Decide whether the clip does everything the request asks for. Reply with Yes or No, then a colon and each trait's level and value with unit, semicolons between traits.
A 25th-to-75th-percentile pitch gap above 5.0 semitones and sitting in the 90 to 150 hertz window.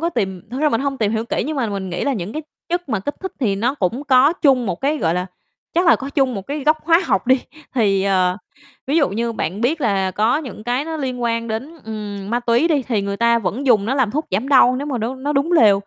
No: wide, 5.5 semitones; high, 245 Hz